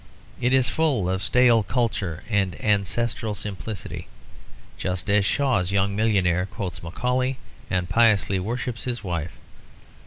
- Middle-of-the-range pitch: No, low, 105 Hz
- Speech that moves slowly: Yes, slow, 125 wpm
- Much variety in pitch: No, average, 4.3 semitones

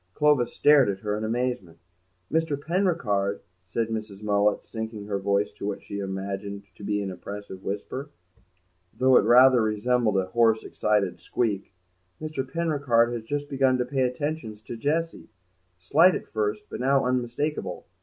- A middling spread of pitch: Yes, average, 4.8 semitones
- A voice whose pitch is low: Yes, low, 115 Hz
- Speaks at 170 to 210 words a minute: No, average, 155 wpm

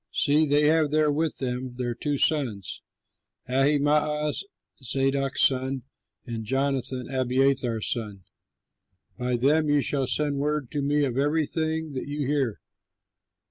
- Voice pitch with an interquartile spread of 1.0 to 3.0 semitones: Yes, average, 2.7 semitones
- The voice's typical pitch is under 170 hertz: Yes, medium, 140 Hz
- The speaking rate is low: Yes, slow, 130 wpm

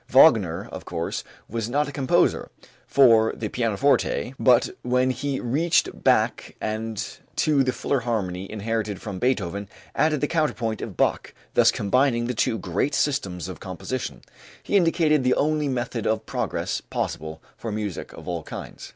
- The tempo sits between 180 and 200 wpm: No, average, 155 wpm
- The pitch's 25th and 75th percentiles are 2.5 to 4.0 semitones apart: No, average, 4.8 semitones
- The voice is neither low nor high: No, low, 120 Hz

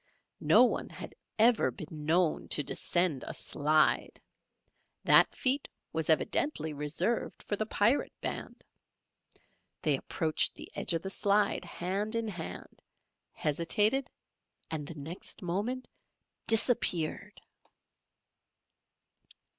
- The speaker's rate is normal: No, slow, 105 wpm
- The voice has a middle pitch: Yes, medium, 180 Hz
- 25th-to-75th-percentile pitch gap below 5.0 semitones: No, wide, 5.6 semitones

